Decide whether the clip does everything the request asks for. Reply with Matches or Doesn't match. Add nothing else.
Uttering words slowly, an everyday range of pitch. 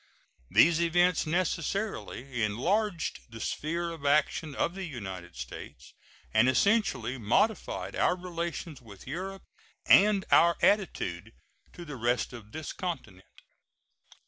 Doesn't match